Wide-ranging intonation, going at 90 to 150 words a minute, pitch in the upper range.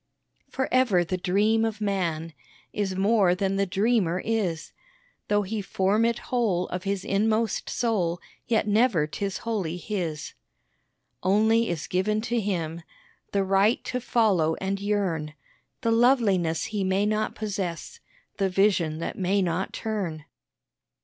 No: average, 3.4 semitones; average, 140 wpm; high, 195 Hz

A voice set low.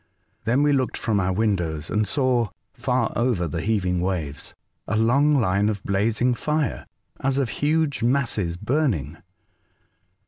Yes: low, 110 Hz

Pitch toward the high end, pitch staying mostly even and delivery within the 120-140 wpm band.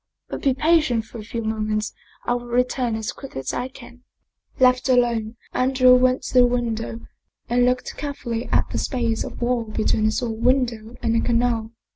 No: high, 240 Hz; narrow, 2.0 semitones; average, 190 wpm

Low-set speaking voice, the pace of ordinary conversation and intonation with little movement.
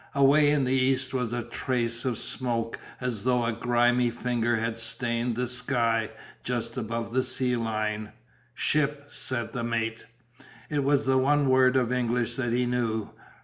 Yes: low, 125 Hz; average, 165 wpm; narrow, 2.0 semitones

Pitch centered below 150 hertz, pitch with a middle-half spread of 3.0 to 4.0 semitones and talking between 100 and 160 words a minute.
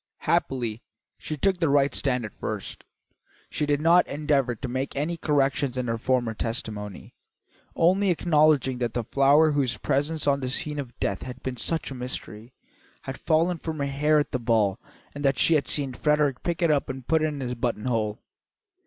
No: low, 135 Hz; average, 3.5 semitones; average, 190 wpm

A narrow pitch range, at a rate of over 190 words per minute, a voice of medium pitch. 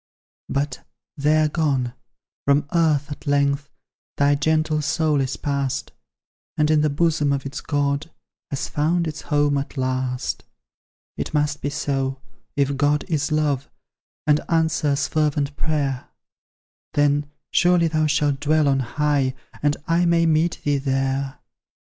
No: narrow, 1.8 semitones; average, 140 wpm; medium, 145 Hz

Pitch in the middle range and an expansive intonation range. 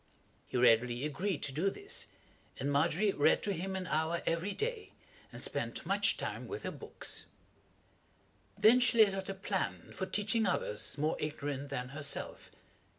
Yes: medium, 170 Hz; wide, 6.0 semitones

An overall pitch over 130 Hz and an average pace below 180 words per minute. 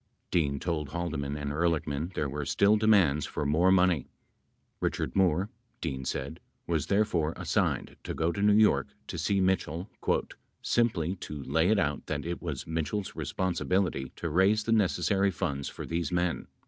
No: very low, 85 Hz; average, 160 wpm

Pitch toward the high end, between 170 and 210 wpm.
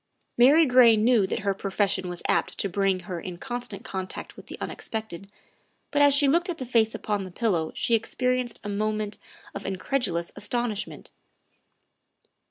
Yes: high, 215 Hz; average, 175 wpm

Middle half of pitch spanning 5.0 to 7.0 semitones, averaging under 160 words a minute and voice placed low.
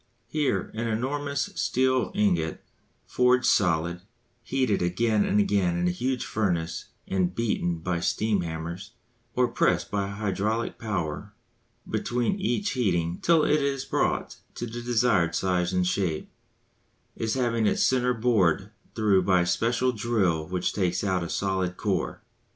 Yes: wide, 5.4 semitones; average, 145 wpm; low, 105 Hz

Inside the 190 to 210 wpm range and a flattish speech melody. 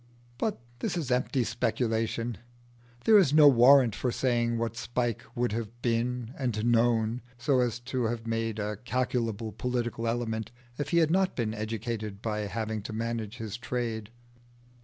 No: average, 160 wpm; narrow, 1.8 semitones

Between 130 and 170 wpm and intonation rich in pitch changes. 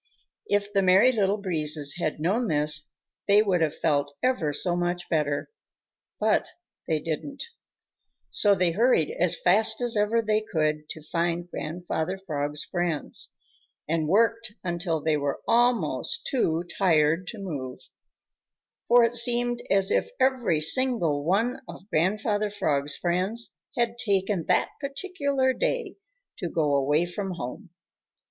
Yes: average, 140 wpm; wide, 6.3 semitones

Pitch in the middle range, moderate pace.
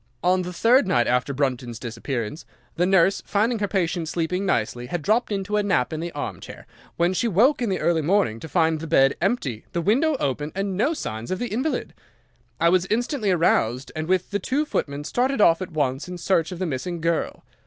No: medium, 175 Hz; fast, 210 wpm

